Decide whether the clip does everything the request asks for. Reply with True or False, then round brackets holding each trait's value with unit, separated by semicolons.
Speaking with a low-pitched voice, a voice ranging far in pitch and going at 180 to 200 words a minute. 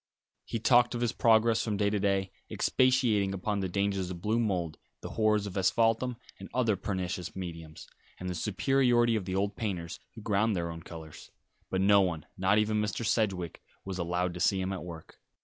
False (100 Hz; 3.4 semitones; 195 wpm)